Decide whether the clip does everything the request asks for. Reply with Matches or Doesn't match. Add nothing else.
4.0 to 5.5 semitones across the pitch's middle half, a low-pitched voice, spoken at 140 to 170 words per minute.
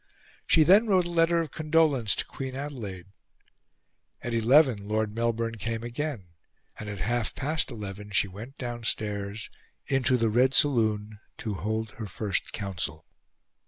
Matches